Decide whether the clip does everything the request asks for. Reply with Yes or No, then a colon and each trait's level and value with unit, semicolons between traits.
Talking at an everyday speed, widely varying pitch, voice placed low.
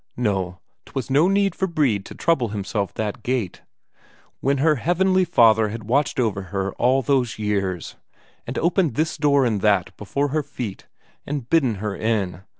Yes: average, 165 wpm; wide, 6.0 semitones; low, 120 Hz